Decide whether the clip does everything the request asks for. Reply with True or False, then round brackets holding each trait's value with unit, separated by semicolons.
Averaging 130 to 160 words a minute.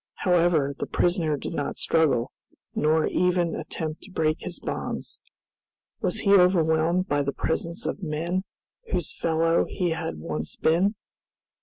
True (140 wpm)